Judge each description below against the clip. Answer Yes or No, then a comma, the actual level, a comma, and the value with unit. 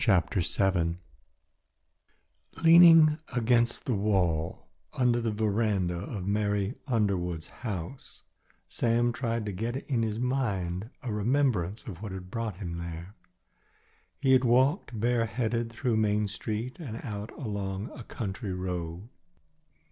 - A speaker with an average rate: No, slow, 125 wpm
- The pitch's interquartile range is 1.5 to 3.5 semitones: No, average, 4.0 semitones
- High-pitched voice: No, low, 110 Hz